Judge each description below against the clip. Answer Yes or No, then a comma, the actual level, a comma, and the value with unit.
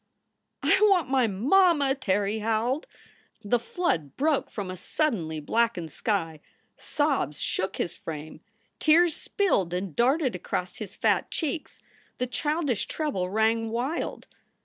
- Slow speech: Yes, slow, 130 wpm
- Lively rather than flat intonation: Yes, wide, 8.1 semitones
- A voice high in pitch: Yes, high, 235 Hz